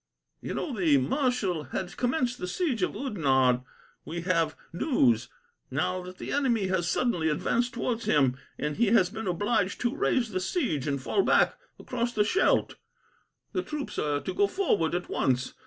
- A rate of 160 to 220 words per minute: Yes, average, 170 wpm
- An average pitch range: No, wide, 8.1 semitones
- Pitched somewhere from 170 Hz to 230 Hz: Yes, medium, 185 Hz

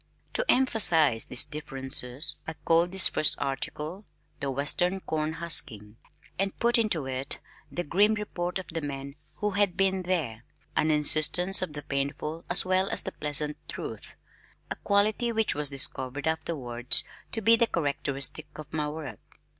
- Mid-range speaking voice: Yes, medium, 160 Hz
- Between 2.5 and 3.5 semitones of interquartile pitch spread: No, average, 5.2 semitones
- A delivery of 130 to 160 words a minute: Yes, average, 155 wpm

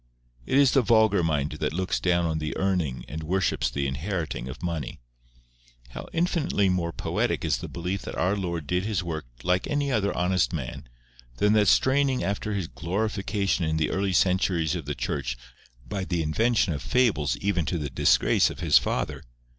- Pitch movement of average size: Yes, average, 4.4 semitones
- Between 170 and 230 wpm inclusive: Yes, average, 185 wpm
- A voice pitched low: Yes, very low, 90 Hz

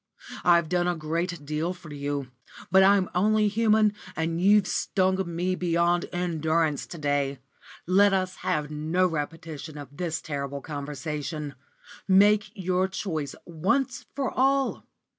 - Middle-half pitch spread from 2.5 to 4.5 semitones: Yes, average, 3.8 semitones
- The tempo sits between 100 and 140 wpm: Yes, slow, 135 wpm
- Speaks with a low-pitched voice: No, medium, 170 Hz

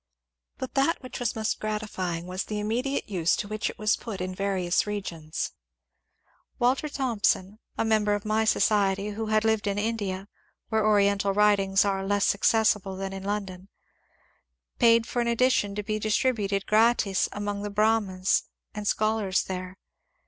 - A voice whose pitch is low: No, high, 210 Hz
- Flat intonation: Yes, narrow, 2.2 semitones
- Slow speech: No, average, 160 wpm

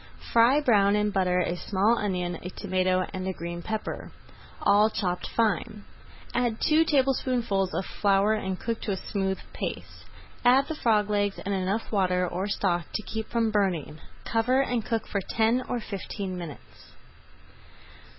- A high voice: Yes, high, 205 Hz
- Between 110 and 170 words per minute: Yes, average, 160 wpm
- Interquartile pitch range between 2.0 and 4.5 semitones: Yes, average, 3.5 semitones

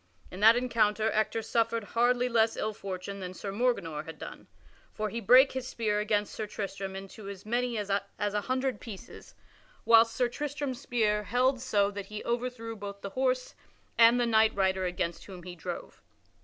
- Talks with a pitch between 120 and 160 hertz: No, high, 220 Hz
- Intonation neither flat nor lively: Yes, average, 3.3 semitones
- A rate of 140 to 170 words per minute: No, average, 180 wpm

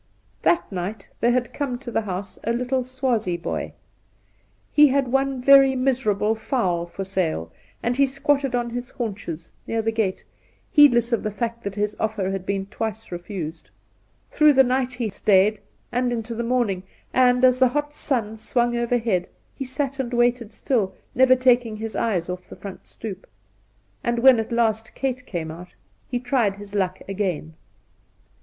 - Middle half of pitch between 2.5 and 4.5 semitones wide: Yes, average, 4.2 semitones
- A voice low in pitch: No, high, 235 Hz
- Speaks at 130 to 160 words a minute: No, average, 175 wpm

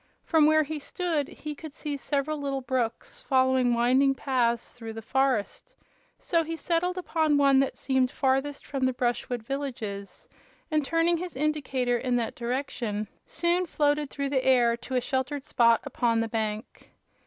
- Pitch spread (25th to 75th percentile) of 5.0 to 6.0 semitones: No, average, 3.6 semitones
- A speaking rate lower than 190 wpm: Yes, average, 165 wpm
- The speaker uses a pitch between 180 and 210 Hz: No, very high, 270 Hz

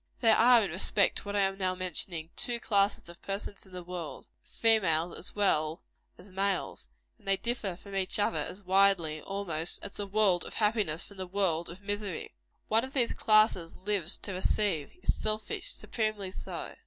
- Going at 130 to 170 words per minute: No, average, 190 wpm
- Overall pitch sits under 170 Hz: No, high, 195 Hz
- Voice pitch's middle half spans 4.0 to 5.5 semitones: No, average, 2.8 semitones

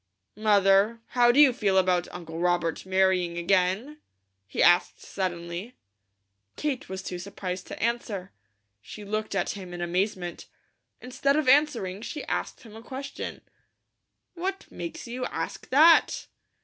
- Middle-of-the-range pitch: No, high, 200 Hz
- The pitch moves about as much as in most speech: No, wide, 5.7 semitones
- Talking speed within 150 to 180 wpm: No, slow, 135 wpm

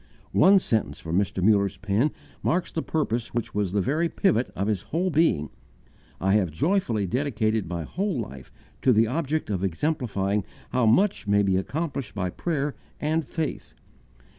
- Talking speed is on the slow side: No, average, 165 wpm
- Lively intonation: Yes, wide, 7.9 semitones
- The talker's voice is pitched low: Yes, low, 110 Hz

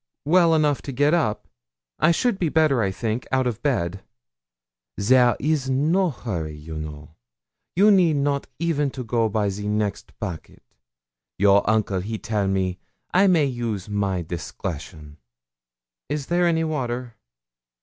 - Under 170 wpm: Yes, average, 145 wpm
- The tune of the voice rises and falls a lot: Yes, wide, 7.3 semitones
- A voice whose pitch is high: No, low, 120 Hz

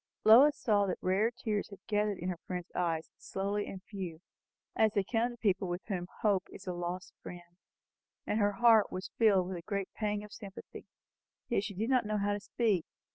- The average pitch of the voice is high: Yes, high, 200 Hz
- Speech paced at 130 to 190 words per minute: No, fast, 205 wpm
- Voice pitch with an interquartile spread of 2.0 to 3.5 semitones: Yes, average, 2.8 semitones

